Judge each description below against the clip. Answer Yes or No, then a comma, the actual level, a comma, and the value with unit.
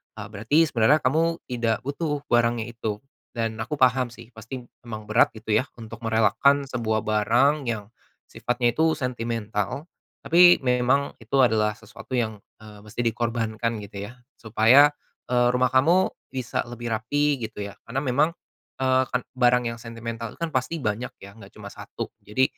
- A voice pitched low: Yes, low, 120 Hz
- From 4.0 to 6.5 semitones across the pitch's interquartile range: No, average, 3.0 semitones